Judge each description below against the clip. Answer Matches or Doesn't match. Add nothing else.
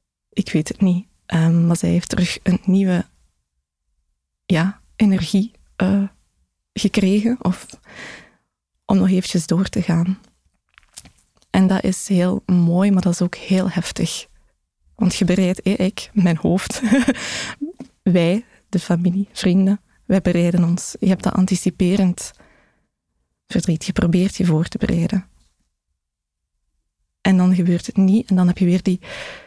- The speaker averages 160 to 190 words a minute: Doesn't match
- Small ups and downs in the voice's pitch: Matches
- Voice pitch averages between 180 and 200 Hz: Matches